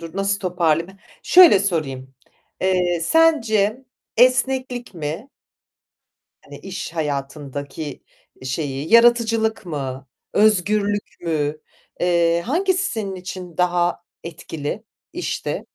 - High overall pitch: No, medium, 180 Hz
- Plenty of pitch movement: Yes, wide, 6.0 semitones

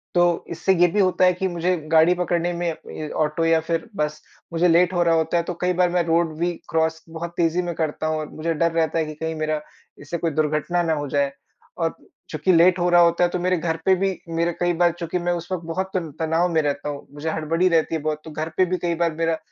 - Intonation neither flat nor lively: No, narrow, 1.7 semitones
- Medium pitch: Yes, medium, 165 Hz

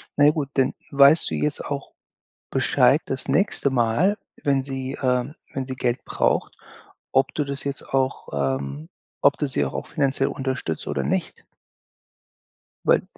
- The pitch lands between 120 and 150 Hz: Yes, low, 135 Hz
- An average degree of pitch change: Yes, average, 3.7 semitones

